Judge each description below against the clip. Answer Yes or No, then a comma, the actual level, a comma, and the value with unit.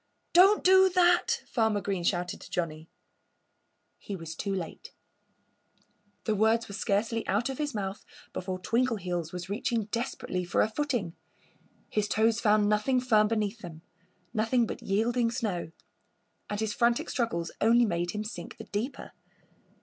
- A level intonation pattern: No, average, 3.7 semitones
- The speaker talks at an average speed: Yes, average, 150 wpm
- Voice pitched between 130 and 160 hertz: No, high, 215 Hz